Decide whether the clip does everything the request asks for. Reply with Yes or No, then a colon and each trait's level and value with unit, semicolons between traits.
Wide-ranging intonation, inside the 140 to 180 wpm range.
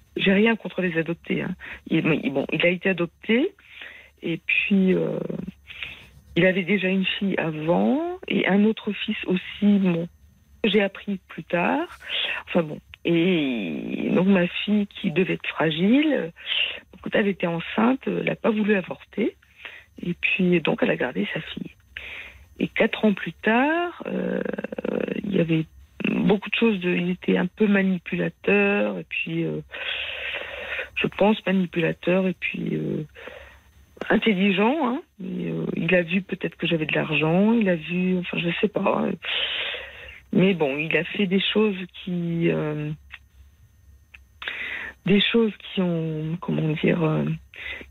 No: average, 4.1 semitones; average, 150 wpm